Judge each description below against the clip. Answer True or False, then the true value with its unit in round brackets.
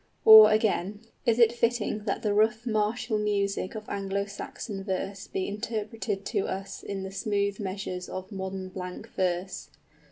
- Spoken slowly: False (155 wpm)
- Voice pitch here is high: True (200 Hz)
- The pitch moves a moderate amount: False (2.0 semitones)